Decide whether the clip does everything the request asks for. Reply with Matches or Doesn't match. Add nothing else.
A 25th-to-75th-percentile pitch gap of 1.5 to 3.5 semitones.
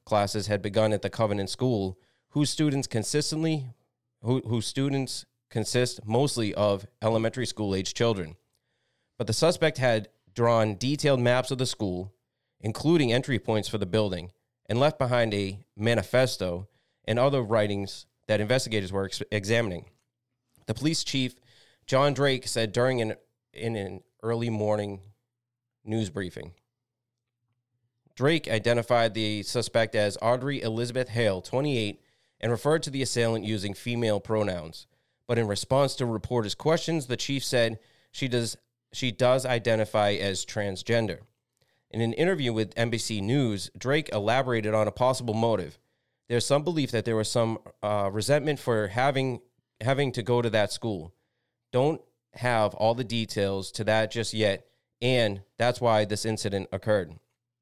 Matches